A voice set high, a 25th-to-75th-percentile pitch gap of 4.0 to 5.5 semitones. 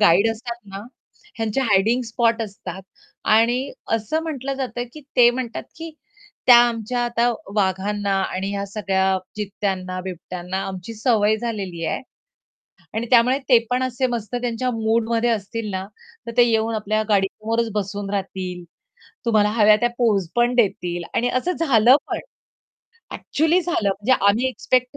No: high, 225 Hz; average, 3.4 semitones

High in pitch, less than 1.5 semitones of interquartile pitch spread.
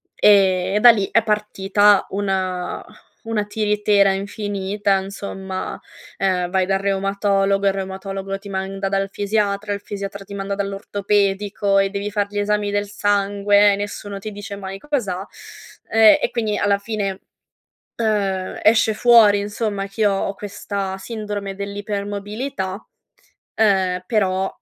Yes: high, 200 Hz; narrow, 1.0 semitones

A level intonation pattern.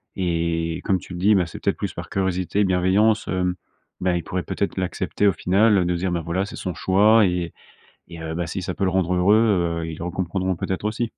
Yes: narrow, 2.1 semitones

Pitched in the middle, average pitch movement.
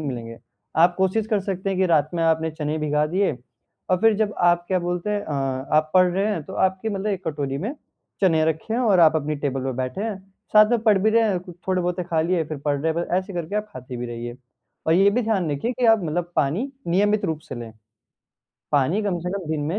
Yes: medium, 175 Hz; average, 4.7 semitones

